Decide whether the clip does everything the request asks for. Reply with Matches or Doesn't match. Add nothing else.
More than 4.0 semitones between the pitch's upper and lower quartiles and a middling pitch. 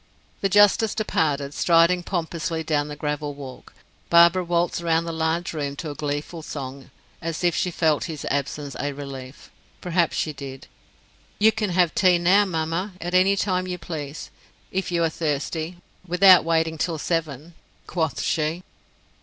Doesn't match